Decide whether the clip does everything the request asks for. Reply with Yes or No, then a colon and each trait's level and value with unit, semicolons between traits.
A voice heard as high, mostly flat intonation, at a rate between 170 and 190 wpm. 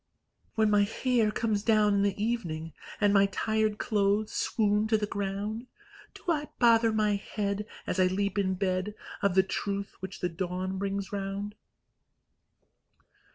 No: high, 205 Hz; narrow, 1.7 semitones; average, 155 wpm